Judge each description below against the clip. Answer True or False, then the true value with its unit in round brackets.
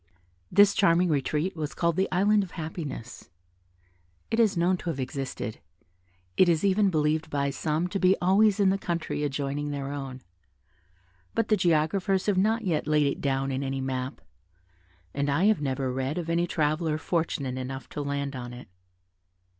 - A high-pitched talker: False (155 Hz)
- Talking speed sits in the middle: True (170 wpm)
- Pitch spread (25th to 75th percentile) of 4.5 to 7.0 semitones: True (5.0 semitones)